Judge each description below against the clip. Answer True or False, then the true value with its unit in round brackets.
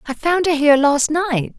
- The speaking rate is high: True (225 wpm)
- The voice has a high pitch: True (300 Hz)